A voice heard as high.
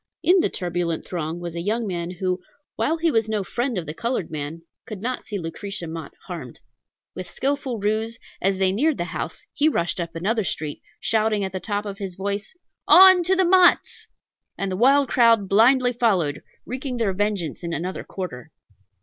Yes: high, 200 Hz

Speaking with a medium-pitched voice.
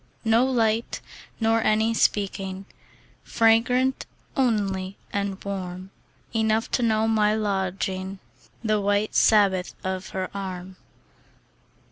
No: high, 205 Hz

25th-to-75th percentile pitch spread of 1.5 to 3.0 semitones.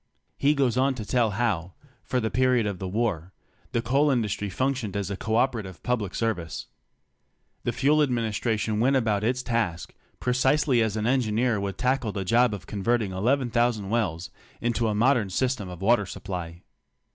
No: average, 3.8 semitones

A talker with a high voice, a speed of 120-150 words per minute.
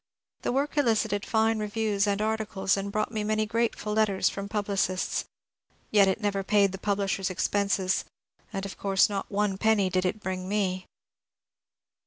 No: high, 205 Hz; average, 165 wpm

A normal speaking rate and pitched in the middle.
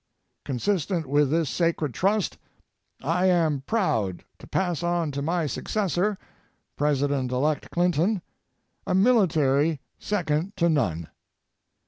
No: slow, 110 wpm; medium, 165 Hz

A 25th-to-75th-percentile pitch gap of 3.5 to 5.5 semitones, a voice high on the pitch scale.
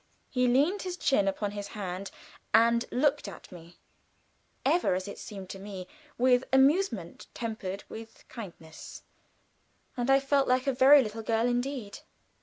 Yes: average, 5.1 semitones; high, 235 Hz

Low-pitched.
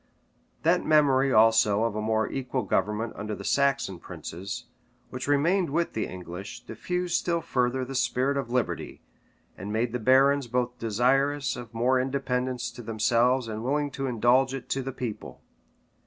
Yes: low, 125 Hz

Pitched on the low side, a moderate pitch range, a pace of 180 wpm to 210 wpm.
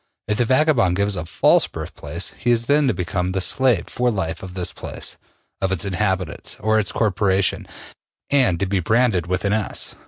Yes: low, 100 Hz; average, 4.3 semitones; average, 190 wpm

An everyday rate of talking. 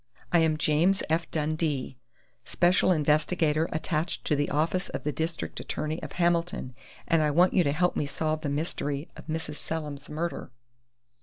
Yes: average, 165 wpm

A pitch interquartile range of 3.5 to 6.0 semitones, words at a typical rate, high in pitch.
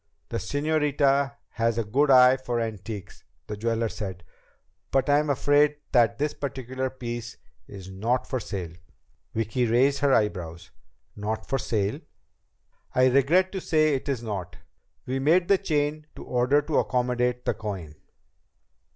No: average, 4.5 semitones; average, 150 wpm; low, 125 Hz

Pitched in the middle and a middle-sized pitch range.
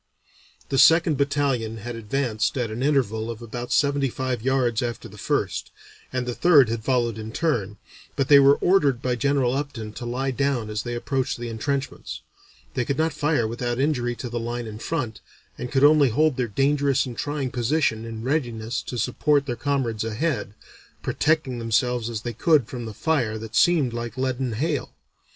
No: low, 125 Hz; average, 3.5 semitones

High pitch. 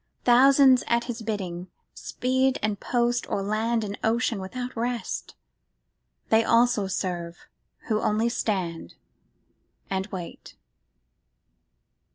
Yes: high, 225 Hz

